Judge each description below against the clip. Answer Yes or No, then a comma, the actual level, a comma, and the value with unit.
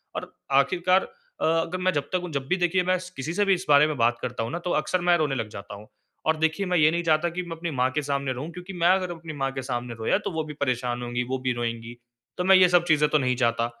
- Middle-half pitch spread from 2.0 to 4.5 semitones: No, wide, 5.6 semitones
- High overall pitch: No, medium, 155 Hz